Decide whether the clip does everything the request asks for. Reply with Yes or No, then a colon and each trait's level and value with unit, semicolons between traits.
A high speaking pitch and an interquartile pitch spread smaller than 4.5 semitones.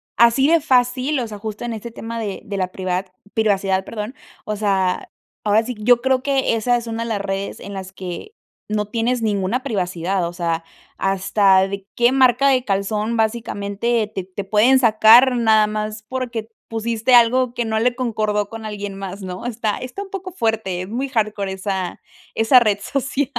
Yes: high, 220 Hz; average, 3.5 semitones